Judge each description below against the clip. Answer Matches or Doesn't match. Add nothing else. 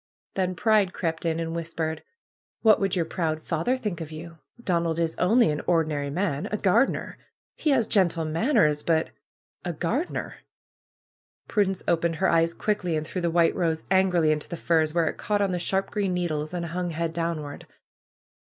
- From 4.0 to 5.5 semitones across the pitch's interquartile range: Doesn't match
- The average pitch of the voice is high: Doesn't match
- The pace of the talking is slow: Doesn't match